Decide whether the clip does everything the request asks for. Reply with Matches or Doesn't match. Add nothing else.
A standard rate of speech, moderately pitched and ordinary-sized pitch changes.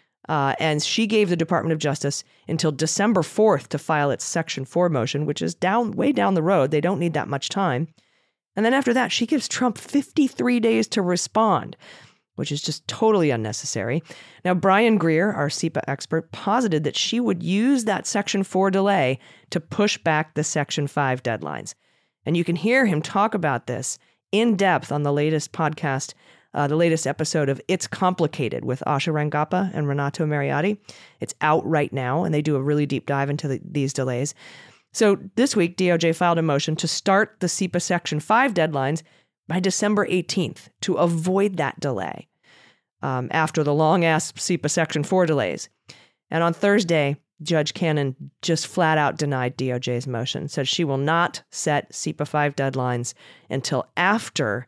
Matches